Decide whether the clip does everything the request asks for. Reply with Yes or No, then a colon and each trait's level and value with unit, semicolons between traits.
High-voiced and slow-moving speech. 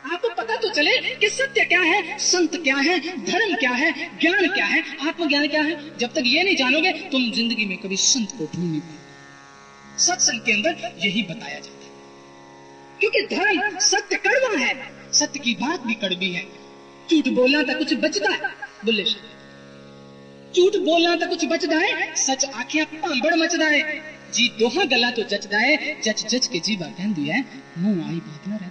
No: very high, 275 Hz; average, 180 wpm